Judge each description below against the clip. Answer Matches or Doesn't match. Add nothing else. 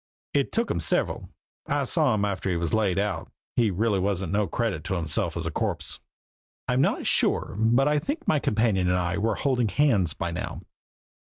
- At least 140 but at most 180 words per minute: Doesn't match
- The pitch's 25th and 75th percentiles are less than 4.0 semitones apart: Doesn't match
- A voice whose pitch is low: Matches